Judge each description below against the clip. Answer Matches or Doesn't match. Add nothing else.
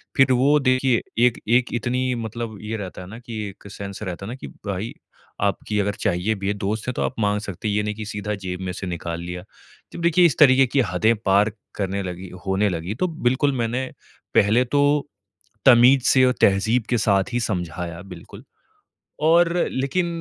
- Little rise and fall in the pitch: Doesn't match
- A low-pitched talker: Matches